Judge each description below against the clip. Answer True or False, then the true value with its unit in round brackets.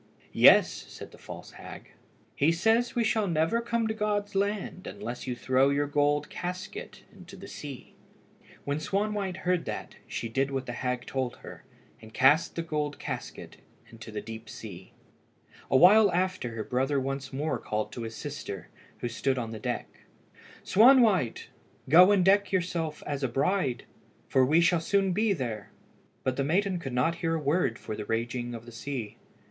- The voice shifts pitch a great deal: True (7.0 semitones)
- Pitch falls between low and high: True (145 Hz)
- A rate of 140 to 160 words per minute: False (175 wpm)